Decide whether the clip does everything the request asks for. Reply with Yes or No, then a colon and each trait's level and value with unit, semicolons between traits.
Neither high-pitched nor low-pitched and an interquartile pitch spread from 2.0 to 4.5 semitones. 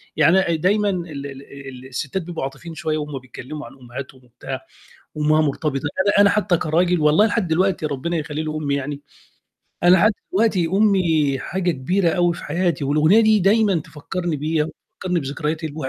Yes: medium, 160 Hz; average, 4.2 semitones